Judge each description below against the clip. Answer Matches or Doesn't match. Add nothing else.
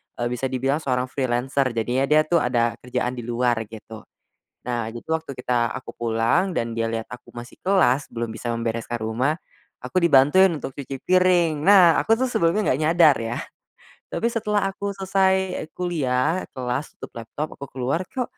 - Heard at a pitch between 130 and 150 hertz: Matches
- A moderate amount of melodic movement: Doesn't match